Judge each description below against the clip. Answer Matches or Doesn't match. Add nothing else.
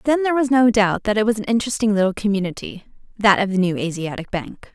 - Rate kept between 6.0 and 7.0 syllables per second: Matches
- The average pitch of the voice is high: Matches